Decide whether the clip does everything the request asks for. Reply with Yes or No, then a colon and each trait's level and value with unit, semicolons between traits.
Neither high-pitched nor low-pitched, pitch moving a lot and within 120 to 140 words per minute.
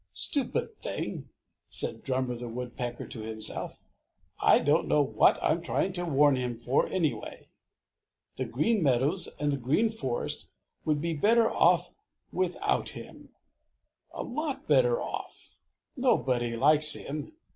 Yes: medium, 150 Hz; wide, 7.1 semitones; slow, 135 wpm